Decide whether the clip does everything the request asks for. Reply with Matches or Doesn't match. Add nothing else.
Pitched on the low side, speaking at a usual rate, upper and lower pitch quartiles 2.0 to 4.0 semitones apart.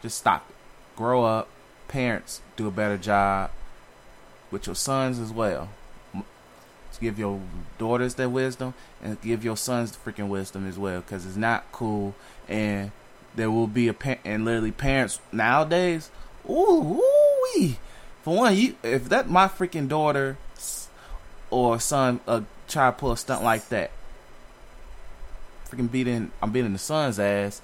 Doesn't match